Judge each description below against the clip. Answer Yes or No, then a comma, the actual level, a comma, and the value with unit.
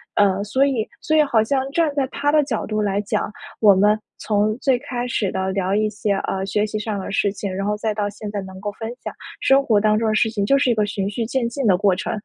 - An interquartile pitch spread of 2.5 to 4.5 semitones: Yes, average, 3.1 semitones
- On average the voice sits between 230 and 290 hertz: No, high, 215 Hz